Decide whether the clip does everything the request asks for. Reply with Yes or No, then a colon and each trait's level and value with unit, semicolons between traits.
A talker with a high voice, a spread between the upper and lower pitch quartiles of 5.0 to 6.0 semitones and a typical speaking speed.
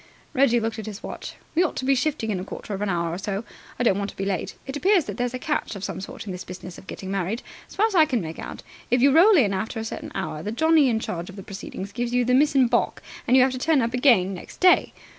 No: high, 230 Hz; wide, 5.6 semitones; fast, 300 wpm